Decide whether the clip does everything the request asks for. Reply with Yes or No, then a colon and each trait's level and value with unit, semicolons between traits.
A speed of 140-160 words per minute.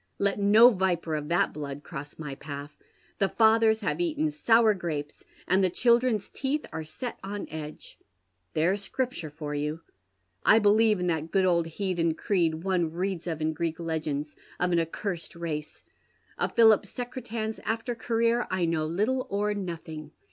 No: average, 170 wpm